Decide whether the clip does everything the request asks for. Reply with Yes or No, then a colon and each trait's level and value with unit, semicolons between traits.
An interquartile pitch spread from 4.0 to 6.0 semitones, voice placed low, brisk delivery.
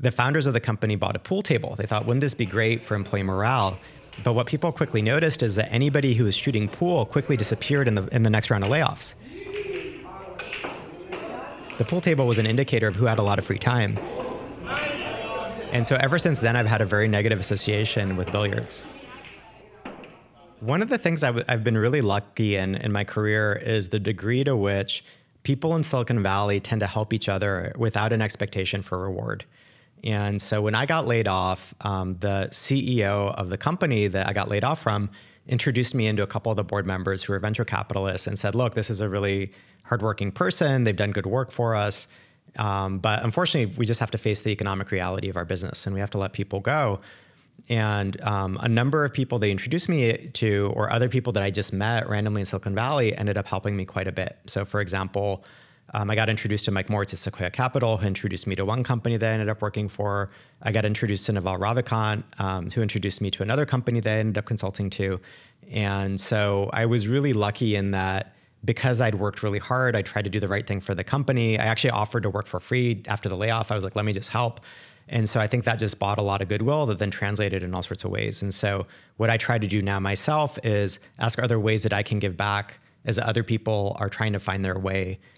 No: average, 3.3 semitones; low, 110 Hz; fast, 230 wpm